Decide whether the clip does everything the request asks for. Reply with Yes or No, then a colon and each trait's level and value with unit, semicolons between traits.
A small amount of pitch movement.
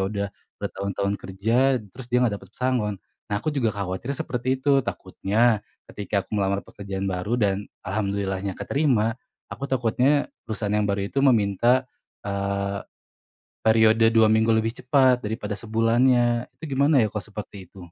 No: average, 3.6 semitones